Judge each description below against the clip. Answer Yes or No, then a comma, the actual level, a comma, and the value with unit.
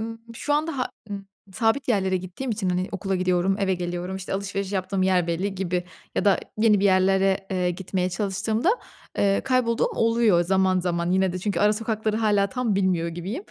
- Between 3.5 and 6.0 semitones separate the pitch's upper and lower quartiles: No, average, 2.8 semitones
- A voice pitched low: No, high, 195 Hz